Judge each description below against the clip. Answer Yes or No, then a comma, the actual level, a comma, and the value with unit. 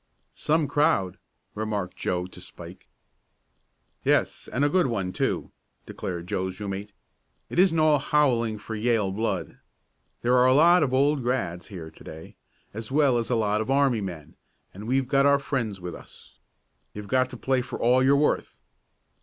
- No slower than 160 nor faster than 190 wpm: Yes, average, 175 wpm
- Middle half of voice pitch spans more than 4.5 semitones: Yes, wide, 5.6 semitones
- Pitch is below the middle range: Yes, low, 120 Hz